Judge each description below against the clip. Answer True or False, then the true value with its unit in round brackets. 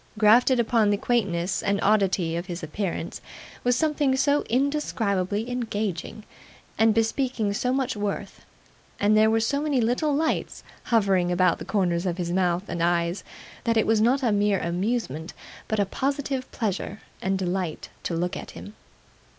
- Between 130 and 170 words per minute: True (160 wpm)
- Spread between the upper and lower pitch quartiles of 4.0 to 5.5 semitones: True (5.1 semitones)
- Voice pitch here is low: False (210 Hz)